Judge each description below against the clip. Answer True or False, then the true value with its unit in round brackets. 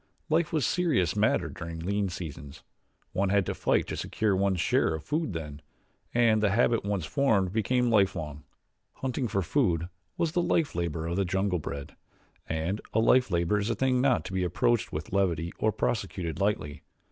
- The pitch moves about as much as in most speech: False (5.7 semitones)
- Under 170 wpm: False (185 wpm)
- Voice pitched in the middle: False (100 Hz)